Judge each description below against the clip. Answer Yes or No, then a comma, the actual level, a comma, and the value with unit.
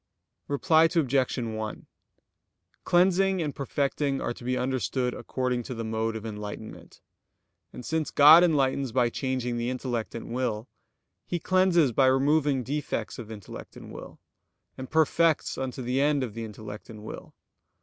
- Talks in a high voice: No, low, 130 Hz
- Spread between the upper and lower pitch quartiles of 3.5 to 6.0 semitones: Yes, average, 4.1 semitones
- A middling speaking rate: Yes, average, 150 wpm